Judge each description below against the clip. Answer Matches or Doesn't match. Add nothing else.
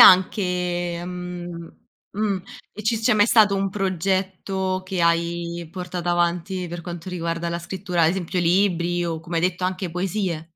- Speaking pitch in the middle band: Matches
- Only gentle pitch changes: Matches